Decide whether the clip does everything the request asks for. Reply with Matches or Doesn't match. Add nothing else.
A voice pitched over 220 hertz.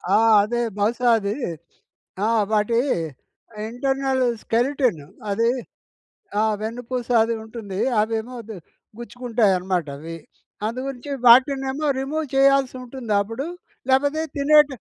Matches